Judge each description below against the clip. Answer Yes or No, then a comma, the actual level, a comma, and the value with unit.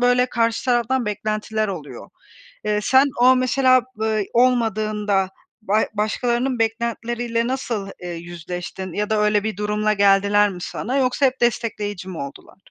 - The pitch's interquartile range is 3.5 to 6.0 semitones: No, average, 2.9 semitones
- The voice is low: No, high, 215 Hz